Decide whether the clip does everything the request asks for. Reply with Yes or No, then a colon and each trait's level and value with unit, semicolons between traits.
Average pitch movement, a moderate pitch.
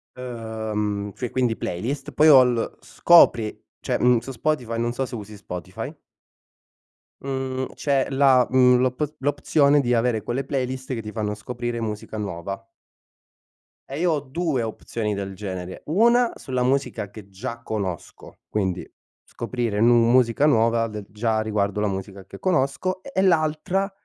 No: average, 4.2 semitones; low, 120 Hz